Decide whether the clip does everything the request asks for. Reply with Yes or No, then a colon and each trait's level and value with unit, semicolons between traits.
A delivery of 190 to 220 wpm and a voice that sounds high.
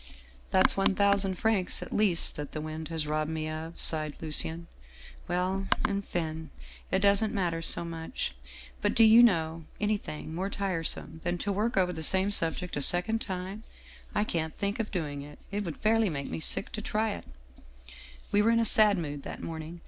No: average, 200 wpm; medium, 175 Hz